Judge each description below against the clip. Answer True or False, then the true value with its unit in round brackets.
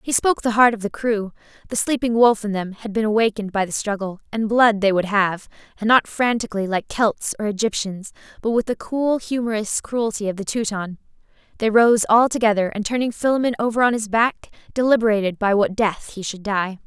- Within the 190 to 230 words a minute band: True (200 wpm)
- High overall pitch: True (215 Hz)